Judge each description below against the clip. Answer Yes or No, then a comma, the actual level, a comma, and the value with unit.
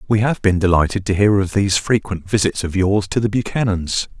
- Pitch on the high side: No, low, 100 Hz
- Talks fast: Yes, fast, 215 wpm